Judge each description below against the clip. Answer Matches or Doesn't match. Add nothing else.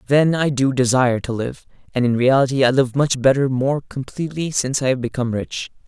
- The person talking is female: Doesn't match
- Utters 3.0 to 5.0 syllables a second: Doesn't match